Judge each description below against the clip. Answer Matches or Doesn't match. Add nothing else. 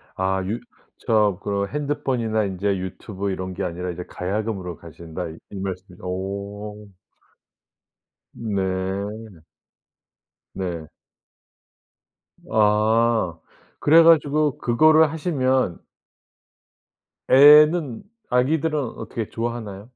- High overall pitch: Doesn't match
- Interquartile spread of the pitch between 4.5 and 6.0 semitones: Matches